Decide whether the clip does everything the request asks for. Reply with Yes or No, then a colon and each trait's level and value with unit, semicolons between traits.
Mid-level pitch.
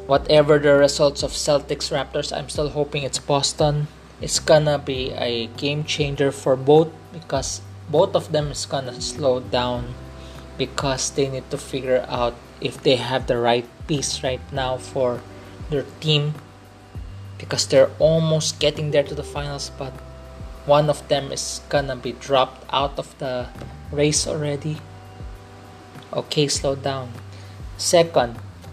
No: low, 130 Hz